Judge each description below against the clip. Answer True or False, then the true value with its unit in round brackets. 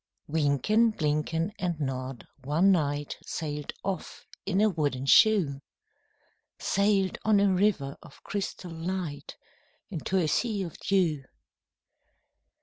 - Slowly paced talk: True (115 wpm)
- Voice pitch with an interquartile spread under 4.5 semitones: False (5.2 semitones)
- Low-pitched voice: False (170 Hz)